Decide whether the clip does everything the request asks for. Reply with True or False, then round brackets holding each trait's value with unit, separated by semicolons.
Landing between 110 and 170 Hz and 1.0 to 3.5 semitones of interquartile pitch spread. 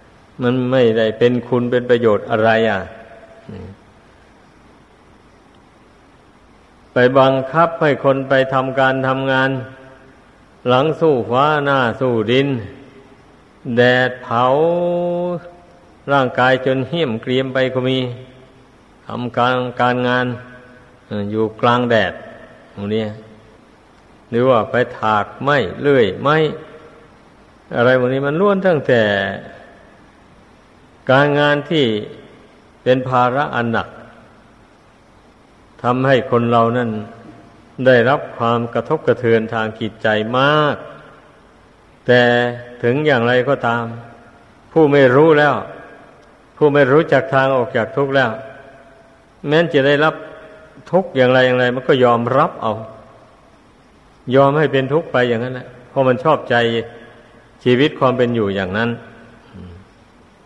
True (125 Hz; 2.6 semitones)